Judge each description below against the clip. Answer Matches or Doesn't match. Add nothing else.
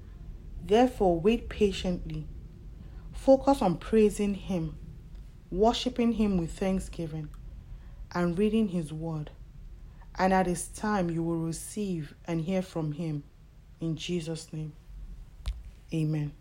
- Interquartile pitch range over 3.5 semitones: Matches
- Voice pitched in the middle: Matches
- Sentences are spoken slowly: Matches